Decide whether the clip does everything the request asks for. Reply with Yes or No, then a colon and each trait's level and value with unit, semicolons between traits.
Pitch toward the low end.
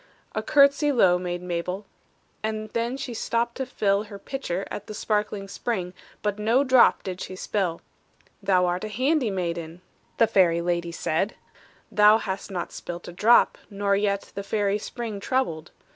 No: high, 200 Hz